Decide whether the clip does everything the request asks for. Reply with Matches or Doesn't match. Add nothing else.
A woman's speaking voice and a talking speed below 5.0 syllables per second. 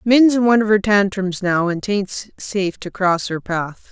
Matches